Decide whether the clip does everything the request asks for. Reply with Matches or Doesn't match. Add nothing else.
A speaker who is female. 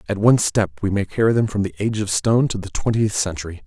Doesn't match